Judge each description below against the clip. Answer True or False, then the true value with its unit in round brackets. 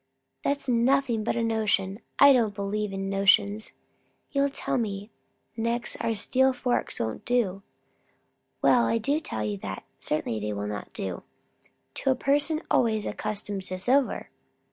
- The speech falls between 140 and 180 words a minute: True (150 wpm)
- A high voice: True (220 Hz)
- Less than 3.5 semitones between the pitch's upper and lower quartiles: False (4.4 semitones)